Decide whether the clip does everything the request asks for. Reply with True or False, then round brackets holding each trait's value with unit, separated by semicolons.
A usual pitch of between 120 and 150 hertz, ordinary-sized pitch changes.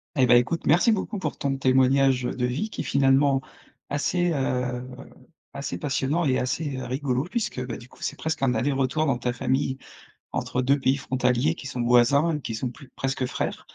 False (135 Hz; 2.3 semitones)